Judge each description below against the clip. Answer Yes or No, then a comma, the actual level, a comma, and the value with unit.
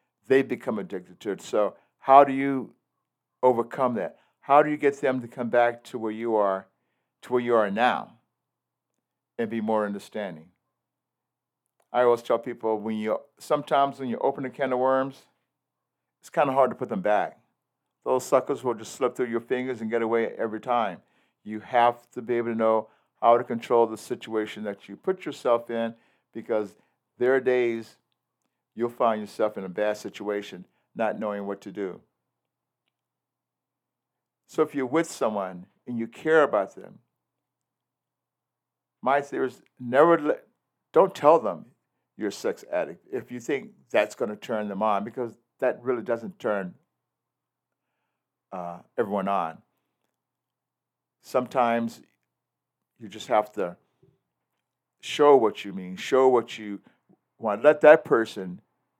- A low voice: Yes, low, 115 Hz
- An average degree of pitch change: Yes, average, 3.0 semitones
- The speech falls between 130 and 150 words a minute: No, average, 160 wpm